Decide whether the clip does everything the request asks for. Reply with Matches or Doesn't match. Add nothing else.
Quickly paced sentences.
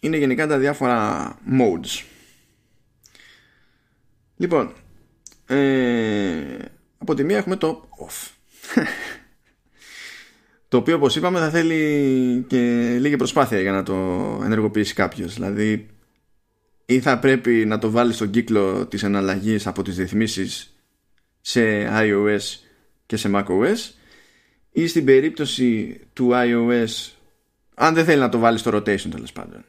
Doesn't match